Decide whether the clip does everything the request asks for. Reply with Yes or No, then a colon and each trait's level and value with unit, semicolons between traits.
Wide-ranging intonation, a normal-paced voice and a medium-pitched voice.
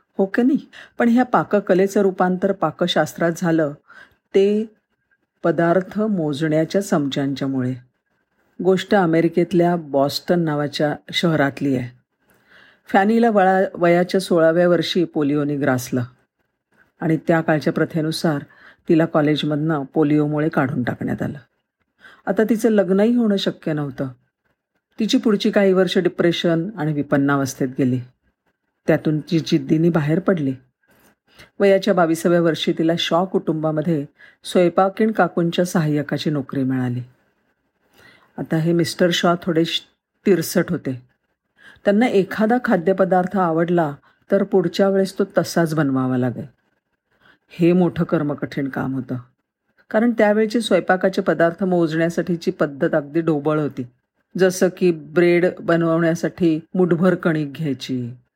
No: average, 4.0 semitones; average, 110 wpm; medium, 170 Hz